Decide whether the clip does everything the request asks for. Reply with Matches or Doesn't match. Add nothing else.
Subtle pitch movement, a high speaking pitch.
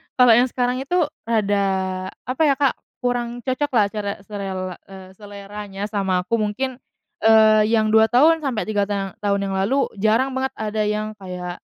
Doesn't match